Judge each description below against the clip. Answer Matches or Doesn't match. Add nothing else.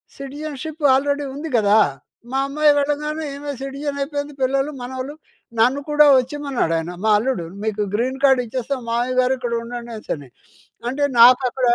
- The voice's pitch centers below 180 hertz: Doesn't match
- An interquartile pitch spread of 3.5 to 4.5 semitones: Doesn't match